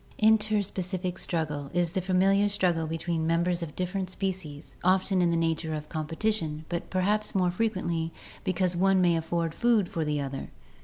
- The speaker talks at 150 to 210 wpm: Yes, average, 165 wpm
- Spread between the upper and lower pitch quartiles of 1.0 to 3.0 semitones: Yes, average, 2.7 semitones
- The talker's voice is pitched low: No, medium, 175 Hz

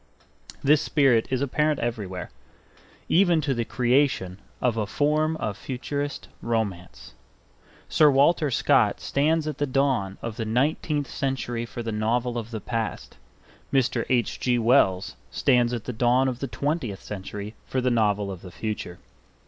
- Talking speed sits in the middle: Yes, average, 155 wpm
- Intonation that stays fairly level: No, average, 4.2 semitones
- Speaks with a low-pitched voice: Yes, low, 125 Hz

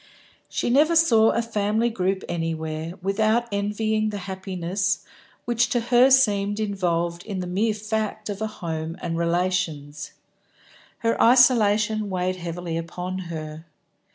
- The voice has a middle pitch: No, high, 200 Hz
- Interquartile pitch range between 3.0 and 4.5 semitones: Yes, average, 4.1 semitones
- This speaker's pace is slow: Yes, slow, 130 wpm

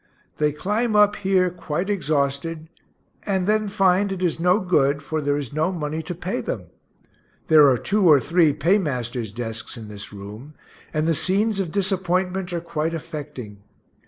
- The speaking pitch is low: No, medium, 165 Hz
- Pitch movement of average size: Yes, average, 4.8 semitones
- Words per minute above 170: No, average, 165 wpm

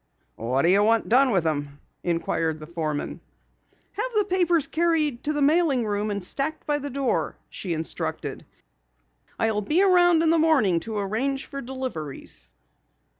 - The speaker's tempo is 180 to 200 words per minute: No, average, 160 wpm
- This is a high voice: Yes, high, 240 Hz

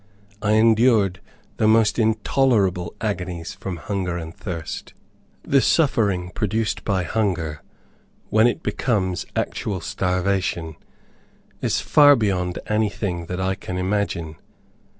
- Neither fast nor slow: No, slow, 110 wpm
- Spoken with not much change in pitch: No, average, 3.5 semitones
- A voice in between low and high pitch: No, very low, 95 Hz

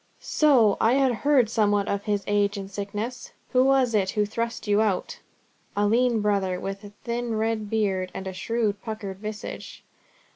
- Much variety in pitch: No, narrow, 2.6 semitones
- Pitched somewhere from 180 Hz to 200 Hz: No, high, 210 Hz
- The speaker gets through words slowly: No, average, 175 wpm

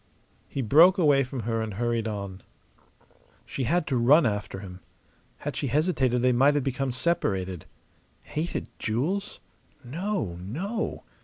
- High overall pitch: No, low, 130 Hz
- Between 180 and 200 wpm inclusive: No, average, 140 wpm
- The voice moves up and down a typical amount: No, wide, 6.0 semitones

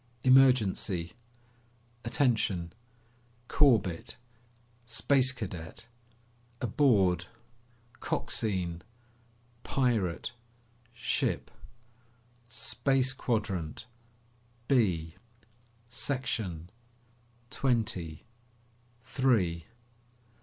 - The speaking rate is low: Yes, slow, 45 wpm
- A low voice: Yes, low, 110 Hz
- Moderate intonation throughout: No, wide, 6.6 semitones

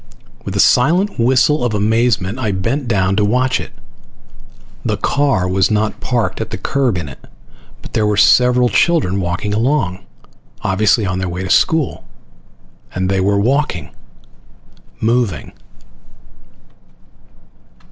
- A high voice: No, low, 110 Hz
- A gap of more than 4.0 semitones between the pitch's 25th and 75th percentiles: Yes, average, 4.9 semitones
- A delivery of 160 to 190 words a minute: No, slow, 135 wpm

